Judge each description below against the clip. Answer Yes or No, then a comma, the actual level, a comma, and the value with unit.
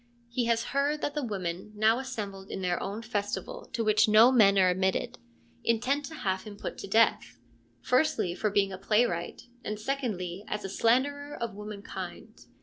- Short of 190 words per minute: Yes, average, 175 wpm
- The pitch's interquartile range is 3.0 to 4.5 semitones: Yes, average, 4.0 semitones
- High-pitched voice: Yes, high, 215 Hz